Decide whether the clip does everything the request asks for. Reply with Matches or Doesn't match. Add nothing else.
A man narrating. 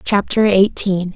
Doesn't match